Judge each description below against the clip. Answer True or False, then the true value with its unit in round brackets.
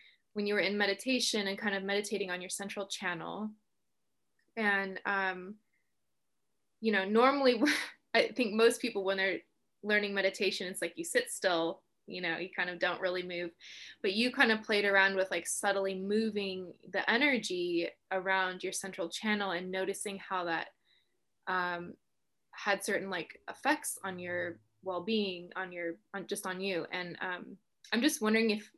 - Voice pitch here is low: False (195 Hz)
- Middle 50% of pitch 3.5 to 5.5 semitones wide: False (2.6 semitones)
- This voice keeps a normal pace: True (165 wpm)